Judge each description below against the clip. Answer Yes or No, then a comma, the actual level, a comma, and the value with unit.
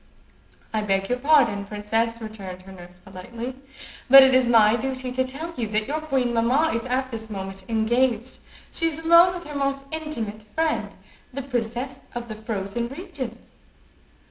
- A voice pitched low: No, high, 240 Hz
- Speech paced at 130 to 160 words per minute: No, average, 170 wpm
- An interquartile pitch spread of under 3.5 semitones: No, average, 4.1 semitones